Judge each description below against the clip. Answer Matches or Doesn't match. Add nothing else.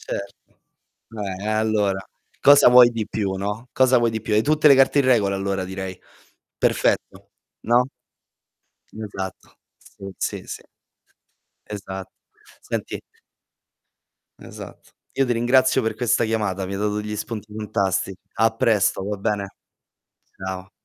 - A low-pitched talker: Matches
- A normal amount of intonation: Matches